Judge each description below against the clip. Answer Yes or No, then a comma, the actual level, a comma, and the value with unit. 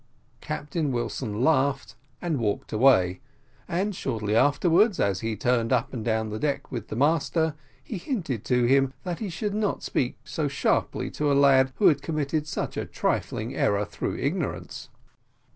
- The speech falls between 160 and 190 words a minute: Yes, average, 165 wpm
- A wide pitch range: Yes, wide, 5.7 semitones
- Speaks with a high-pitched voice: No, low, 135 Hz